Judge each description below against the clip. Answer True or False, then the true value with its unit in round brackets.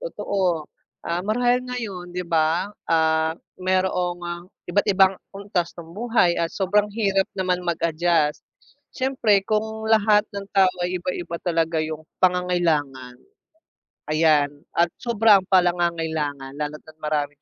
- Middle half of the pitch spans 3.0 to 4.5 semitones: True (3.5 semitones)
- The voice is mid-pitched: True (175 Hz)